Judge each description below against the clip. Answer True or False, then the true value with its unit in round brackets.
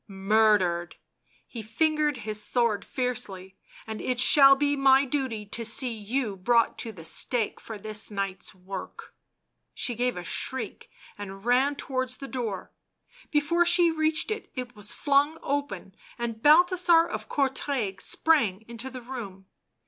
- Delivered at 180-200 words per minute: False (155 wpm)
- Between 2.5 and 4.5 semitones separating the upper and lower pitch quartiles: False (5.1 semitones)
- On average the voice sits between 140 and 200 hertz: False (245 Hz)